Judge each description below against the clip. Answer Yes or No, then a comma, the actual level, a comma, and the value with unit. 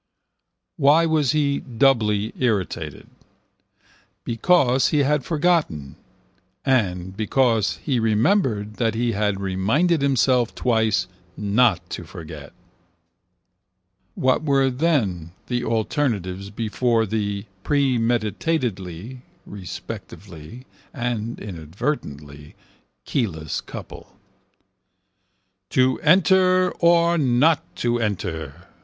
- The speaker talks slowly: Yes, slow, 85 wpm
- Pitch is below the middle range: Yes, low, 115 Hz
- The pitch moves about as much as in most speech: No, wide, 6.0 semitones